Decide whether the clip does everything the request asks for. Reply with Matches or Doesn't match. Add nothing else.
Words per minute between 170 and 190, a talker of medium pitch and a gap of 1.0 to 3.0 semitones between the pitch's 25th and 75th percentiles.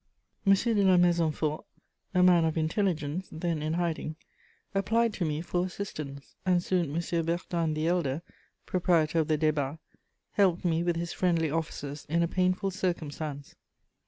Doesn't match